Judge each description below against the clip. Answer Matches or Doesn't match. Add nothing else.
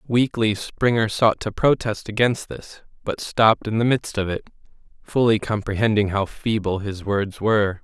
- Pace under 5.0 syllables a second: Matches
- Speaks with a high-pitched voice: Doesn't match